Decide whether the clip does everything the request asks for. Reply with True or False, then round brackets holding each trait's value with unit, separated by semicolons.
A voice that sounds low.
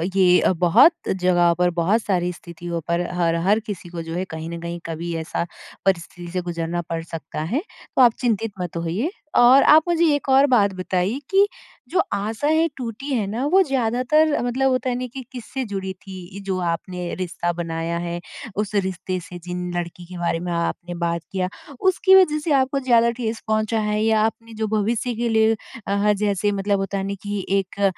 False (195 Hz)